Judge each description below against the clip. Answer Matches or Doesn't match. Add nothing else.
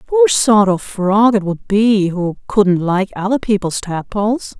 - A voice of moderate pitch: Doesn't match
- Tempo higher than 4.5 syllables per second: Doesn't match